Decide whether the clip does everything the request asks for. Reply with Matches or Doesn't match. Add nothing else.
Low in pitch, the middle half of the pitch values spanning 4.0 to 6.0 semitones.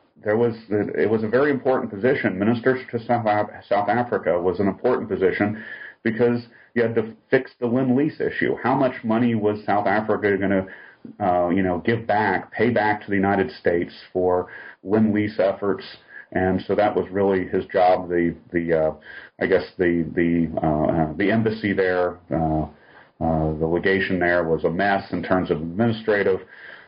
Matches